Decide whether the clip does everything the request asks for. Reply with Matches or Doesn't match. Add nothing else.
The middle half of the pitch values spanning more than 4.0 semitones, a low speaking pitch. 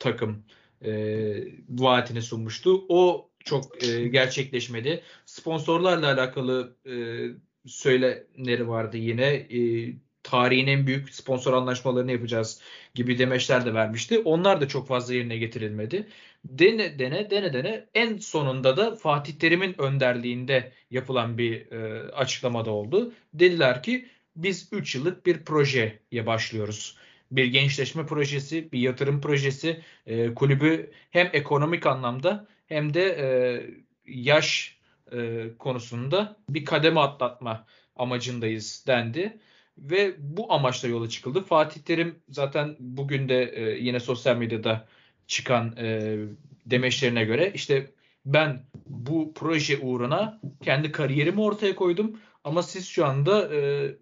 Matches